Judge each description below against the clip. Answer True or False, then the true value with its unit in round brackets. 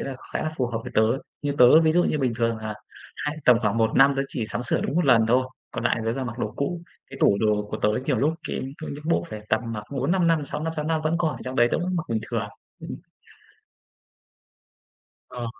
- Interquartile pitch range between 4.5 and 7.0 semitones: True (5.2 semitones)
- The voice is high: False (130 Hz)